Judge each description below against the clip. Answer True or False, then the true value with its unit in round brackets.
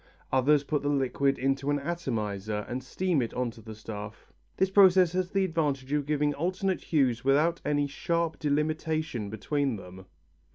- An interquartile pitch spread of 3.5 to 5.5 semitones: True (4.7 semitones)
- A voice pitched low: False (145 Hz)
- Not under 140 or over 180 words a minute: True (165 wpm)